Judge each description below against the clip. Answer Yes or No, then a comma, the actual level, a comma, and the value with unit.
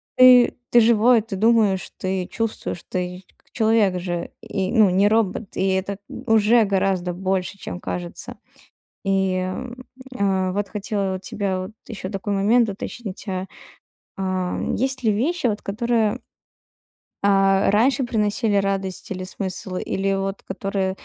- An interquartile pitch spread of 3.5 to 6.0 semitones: No, average, 2.9 semitones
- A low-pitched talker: No, high, 195 Hz